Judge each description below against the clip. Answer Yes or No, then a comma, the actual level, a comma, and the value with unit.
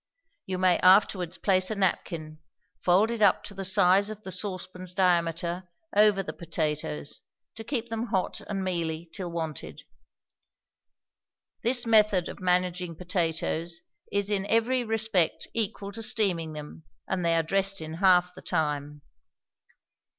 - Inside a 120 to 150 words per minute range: Yes, average, 140 wpm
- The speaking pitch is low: No, medium, 185 Hz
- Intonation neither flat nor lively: Yes, average, 3.3 semitones